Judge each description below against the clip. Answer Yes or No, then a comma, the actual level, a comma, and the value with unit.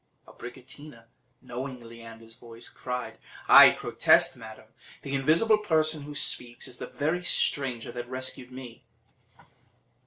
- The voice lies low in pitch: Yes, low, 130 Hz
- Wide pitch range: No, average, 3.3 semitones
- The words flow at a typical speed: No, slow, 120 wpm